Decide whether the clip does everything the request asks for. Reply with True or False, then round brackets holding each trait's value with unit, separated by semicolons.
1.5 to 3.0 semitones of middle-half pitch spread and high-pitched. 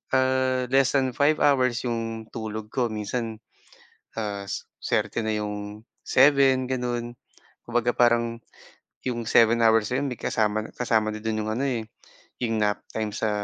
False (2.7 semitones; 115 Hz)